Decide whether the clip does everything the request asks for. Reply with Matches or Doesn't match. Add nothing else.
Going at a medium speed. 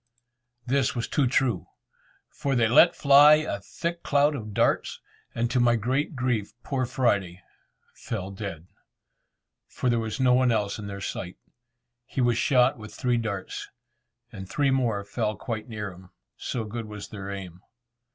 Matches